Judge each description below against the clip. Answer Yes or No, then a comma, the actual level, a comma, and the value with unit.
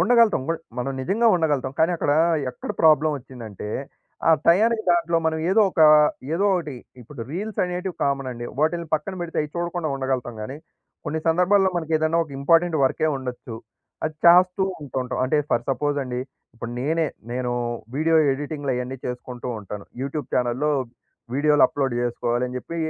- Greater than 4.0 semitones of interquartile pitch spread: Yes, average, 4.8 semitones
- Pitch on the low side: No, medium, 150 Hz